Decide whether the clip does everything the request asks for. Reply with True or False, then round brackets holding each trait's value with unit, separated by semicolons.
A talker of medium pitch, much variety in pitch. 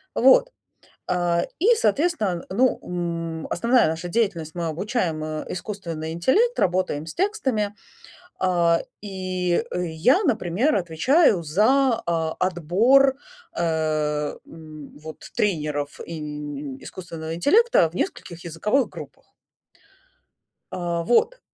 True (175 Hz; 6.3 semitones)